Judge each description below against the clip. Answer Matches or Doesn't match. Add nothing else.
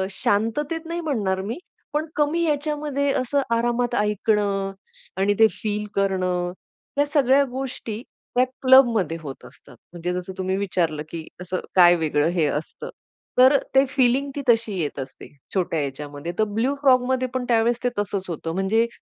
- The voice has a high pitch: Matches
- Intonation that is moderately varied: Doesn't match